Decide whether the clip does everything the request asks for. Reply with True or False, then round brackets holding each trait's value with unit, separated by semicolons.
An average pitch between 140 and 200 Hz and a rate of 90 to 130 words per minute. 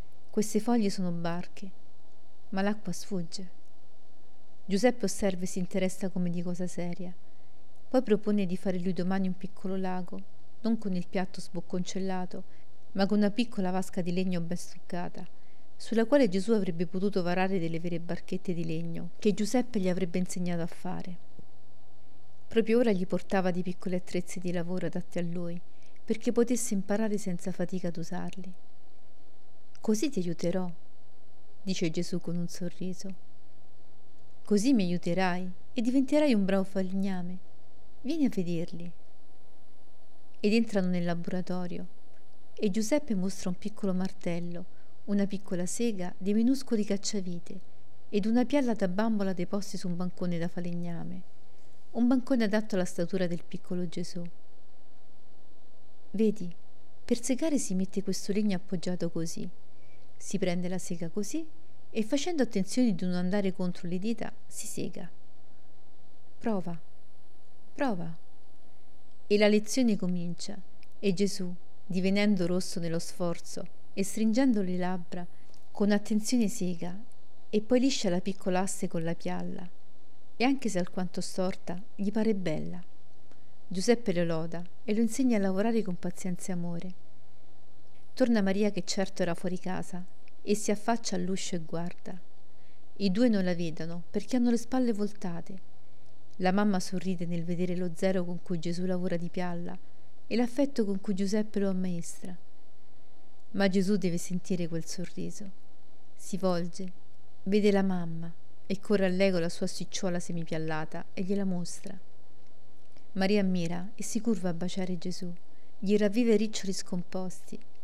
False (185 Hz; 140 wpm)